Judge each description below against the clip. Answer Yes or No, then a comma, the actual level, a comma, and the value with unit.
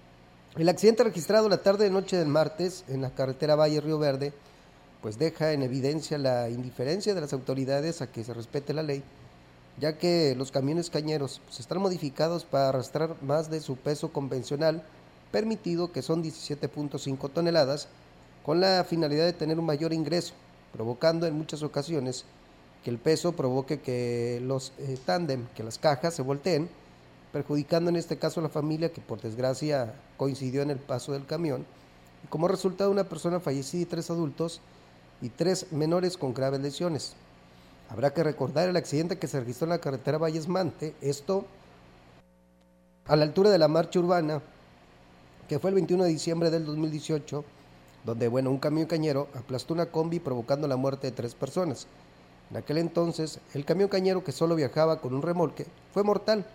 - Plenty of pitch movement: No, average, 4.5 semitones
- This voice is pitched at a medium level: Yes, medium, 150 Hz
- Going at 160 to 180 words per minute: Yes, average, 170 wpm